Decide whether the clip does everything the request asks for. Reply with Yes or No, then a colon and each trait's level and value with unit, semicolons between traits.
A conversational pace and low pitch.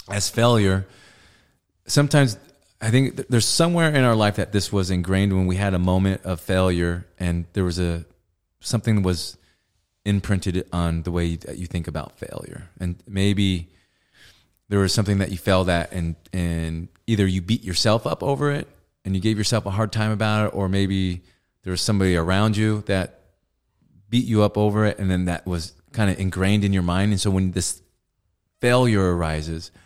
Yes: average, 185 wpm; very low, 95 Hz